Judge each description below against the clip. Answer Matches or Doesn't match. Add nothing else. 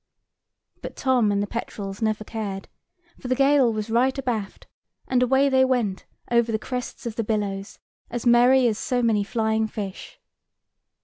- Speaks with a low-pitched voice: Doesn't match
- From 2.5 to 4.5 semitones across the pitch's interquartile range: Matches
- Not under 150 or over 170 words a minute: Matches